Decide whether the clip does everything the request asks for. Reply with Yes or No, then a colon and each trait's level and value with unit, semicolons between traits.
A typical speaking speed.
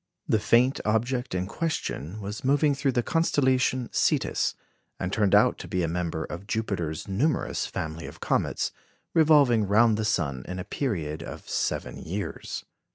Yes: average, 160 wpm